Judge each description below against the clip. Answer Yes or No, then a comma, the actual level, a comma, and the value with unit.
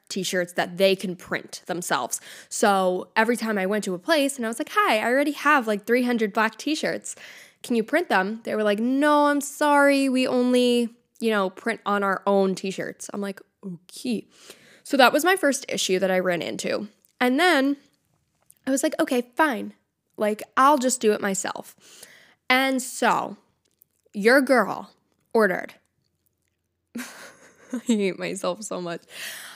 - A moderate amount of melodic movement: No, wide, 5.9 semitones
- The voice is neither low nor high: No, high, 230 Hz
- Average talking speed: Yes, average, 170 wpm